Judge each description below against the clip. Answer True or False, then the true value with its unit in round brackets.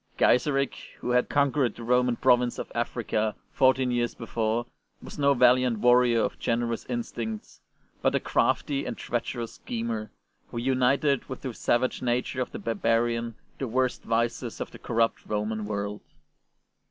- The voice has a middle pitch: False (120 Hz)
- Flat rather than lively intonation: True (1.8 semitones)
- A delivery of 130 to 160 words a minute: True (150 wpm)